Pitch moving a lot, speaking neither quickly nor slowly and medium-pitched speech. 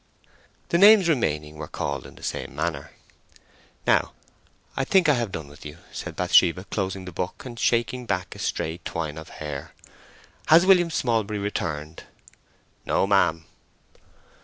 No: wide, 7.9 semitones; average, 150 wpm; very low, 95 Hz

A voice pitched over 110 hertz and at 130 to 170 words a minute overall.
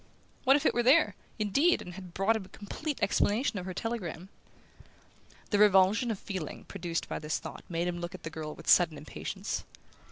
No: high, 190 Hz; average, 195 wpm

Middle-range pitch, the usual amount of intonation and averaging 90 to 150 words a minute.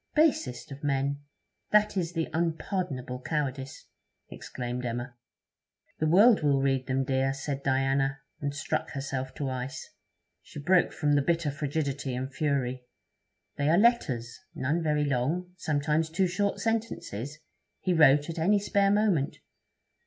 Yes: medium, 145 Hz; average, 4.1 semitones; average, 140 wpm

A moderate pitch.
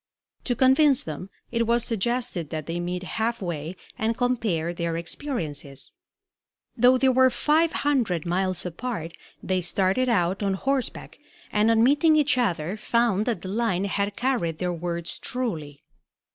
No: high, 205 Hz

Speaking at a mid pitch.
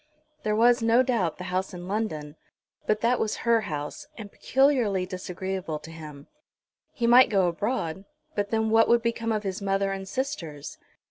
No: high, 200 Hz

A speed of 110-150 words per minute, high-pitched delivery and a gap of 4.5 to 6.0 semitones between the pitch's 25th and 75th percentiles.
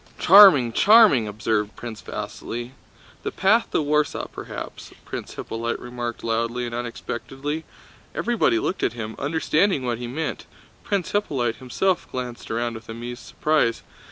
No: slow, 135 wpm; low, 125 Hz; wide, 5.4 semitones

